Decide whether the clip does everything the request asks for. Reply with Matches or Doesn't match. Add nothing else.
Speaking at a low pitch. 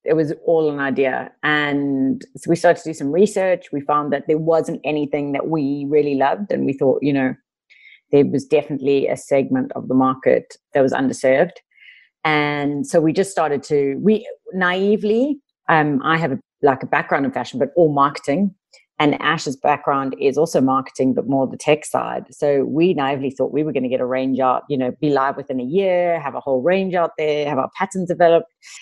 Doesn't match